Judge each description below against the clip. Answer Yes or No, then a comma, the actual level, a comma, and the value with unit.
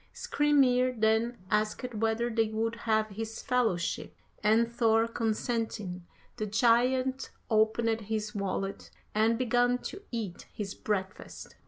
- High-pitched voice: Yes, high, 225 Hz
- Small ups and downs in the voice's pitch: Yes, narrow, 2.1 semitones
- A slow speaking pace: Yes, slow, 120 wpm